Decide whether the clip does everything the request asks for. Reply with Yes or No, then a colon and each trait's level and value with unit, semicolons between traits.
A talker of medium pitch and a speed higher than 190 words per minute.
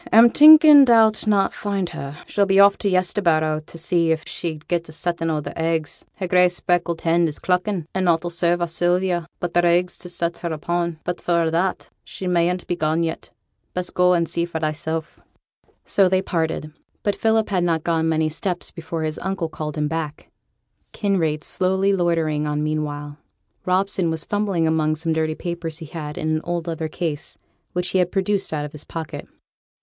Yes: medium, 170 Hz; average, 200 wpm